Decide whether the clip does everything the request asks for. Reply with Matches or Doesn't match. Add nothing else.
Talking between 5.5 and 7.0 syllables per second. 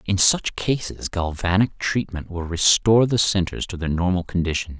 Doesn't match